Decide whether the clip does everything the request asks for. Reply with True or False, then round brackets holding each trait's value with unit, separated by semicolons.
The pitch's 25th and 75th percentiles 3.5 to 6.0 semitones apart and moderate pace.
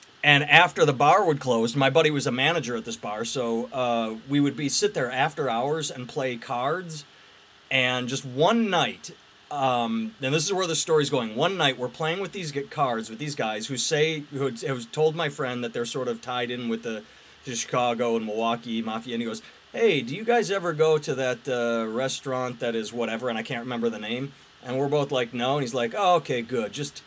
False (4.6 semitones; 230 wpm)